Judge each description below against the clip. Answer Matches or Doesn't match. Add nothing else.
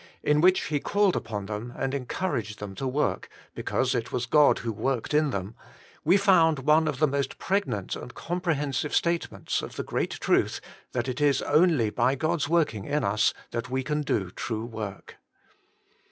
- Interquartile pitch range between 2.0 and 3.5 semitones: Doesn't match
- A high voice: Doesn't match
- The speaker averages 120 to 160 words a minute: Doesn't match